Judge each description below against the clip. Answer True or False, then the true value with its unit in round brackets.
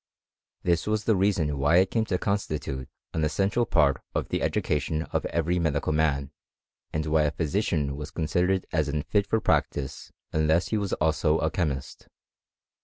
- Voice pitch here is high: False (80 Hz)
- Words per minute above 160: True (170 wpm)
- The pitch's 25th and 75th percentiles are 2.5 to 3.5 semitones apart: False (4.1 semitones)